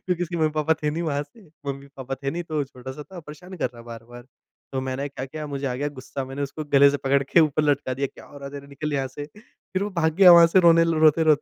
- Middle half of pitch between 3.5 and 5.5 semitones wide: No, average, 2.9 semitones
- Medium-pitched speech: Yes, medium, 145 Hz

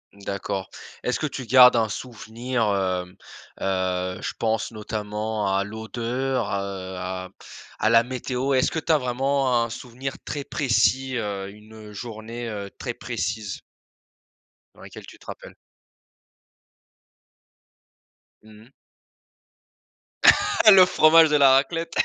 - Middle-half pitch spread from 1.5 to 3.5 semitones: No, average, 4.3 semitones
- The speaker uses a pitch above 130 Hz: No, low, 115 Hz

